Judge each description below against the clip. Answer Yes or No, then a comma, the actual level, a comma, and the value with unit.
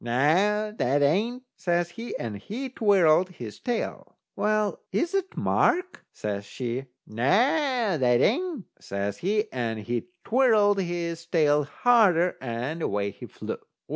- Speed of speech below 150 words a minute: Yes, slow, 135 wpm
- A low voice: No, medium, 175 Hz